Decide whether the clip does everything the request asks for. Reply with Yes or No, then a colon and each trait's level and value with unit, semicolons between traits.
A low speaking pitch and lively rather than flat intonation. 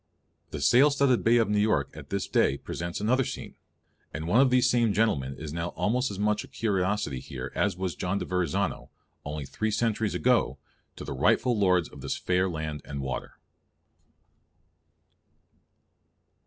Yes: low, 100 Hz; wide, 6.4 semitones